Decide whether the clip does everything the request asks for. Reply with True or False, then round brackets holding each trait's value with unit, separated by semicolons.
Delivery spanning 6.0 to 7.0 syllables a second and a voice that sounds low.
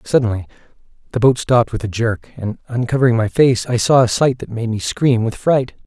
False (5.5 syllables/s; 120 Hz)